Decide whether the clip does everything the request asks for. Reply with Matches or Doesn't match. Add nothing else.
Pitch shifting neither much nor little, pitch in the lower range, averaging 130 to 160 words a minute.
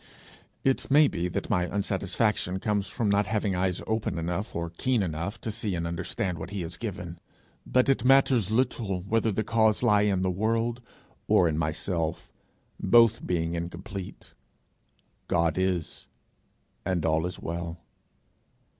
Matches